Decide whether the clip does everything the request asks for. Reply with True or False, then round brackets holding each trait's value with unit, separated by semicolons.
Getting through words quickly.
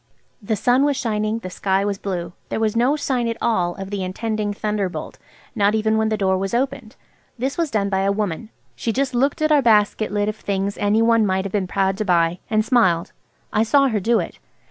True (225 wpm)